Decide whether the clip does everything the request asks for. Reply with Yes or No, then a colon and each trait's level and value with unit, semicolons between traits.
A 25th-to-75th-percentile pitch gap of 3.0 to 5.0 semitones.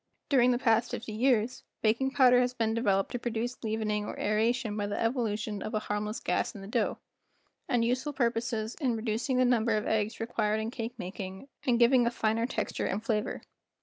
No: narrow, 2.4 semitones